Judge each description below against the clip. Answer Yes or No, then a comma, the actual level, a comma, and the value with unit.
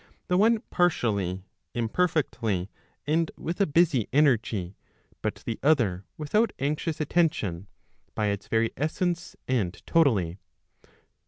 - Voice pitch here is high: No, low, 130 Hz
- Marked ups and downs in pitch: Yes, wide, 8.2 semitones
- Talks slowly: Yes, slow, 110 wpm